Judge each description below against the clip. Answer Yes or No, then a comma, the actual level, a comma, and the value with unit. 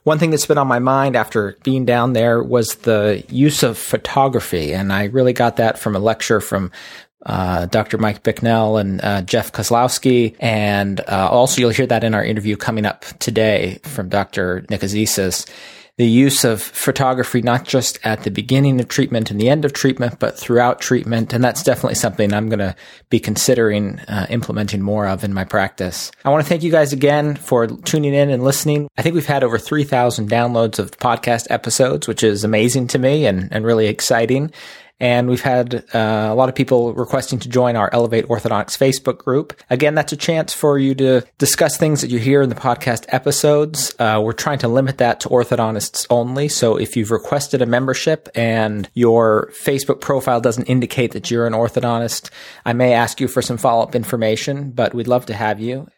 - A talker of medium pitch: No, low, 120 Hz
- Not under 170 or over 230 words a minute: Yes, average, 200 wpm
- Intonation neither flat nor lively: Yes, average, 3.6 semitones